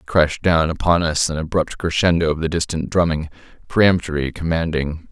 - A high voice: No, very low, 80 Hz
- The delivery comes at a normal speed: Yes, average, 155 wpm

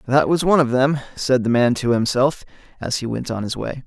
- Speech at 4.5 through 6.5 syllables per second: Yes, 5.6 syllables/s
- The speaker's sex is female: No, male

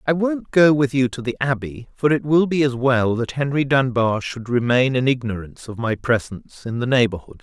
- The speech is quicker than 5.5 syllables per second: No, 5.3 syllables/s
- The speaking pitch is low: Yes, low, 130 Hz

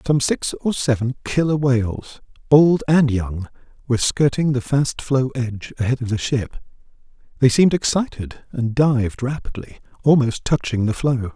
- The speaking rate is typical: Yes, average, 155 wpm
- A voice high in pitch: No, low, 125 Hz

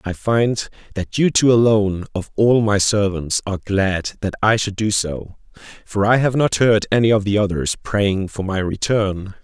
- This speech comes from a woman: No, male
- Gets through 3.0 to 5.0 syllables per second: Yes, 4.5 syllables/s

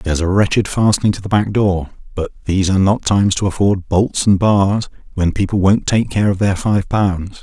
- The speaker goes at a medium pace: No, fast, 220 wpm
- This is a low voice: Yes, low, 100 Hz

